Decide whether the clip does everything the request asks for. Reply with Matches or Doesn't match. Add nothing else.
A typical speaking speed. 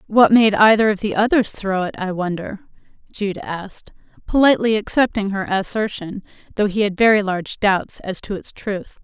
Matches